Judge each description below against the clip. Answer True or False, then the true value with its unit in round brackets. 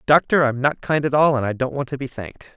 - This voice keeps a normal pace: False (305 wpm)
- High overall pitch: False (135 Hz)